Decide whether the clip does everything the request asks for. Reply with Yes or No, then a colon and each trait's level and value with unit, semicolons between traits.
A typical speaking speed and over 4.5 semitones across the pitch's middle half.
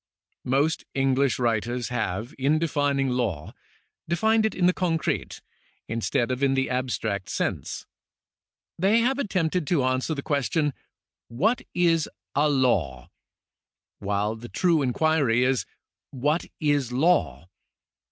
No: slow, 130 wpm; average, 5.2 semitones